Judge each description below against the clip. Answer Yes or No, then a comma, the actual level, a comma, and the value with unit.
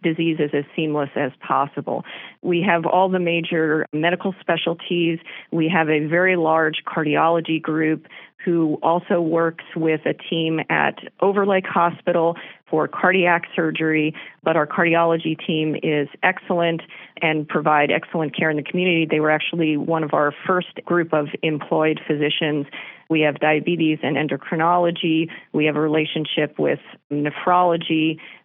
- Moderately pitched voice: Yes, medium, 160 Hz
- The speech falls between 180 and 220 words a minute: No, average, 140 wpm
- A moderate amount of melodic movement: No, narrow, 1.8 semitones